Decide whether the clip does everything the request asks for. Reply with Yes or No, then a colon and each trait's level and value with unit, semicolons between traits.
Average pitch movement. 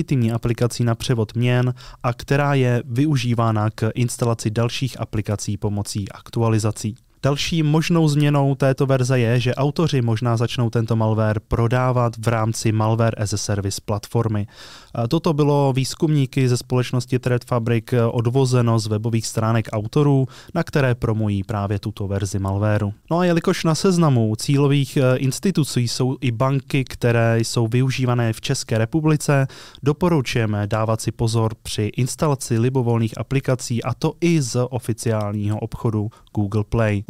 Yes: average, 3.3 semitones